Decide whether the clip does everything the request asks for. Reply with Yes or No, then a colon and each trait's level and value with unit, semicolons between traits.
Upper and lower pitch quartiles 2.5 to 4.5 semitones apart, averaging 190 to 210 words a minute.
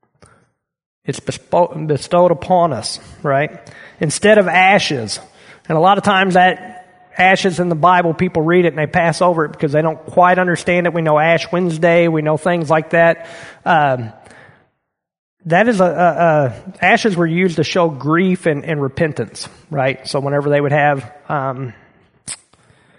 No: average, 3.0 semitones; average, 165 wpm